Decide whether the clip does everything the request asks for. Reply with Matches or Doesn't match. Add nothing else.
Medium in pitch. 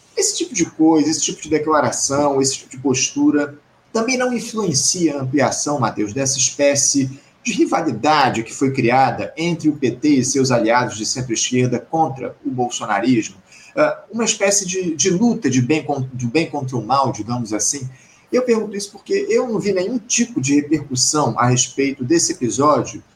Matches